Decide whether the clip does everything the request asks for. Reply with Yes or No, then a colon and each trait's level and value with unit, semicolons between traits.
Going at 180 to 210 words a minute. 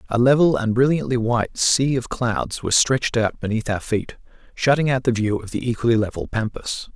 Yes: average, 200 wpm